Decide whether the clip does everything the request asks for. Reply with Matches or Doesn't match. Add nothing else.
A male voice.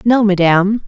Doesn't match